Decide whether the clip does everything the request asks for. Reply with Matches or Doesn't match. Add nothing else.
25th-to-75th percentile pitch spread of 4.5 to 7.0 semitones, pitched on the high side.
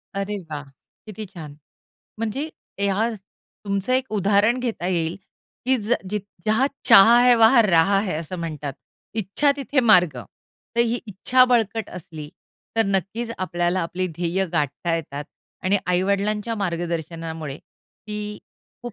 Matches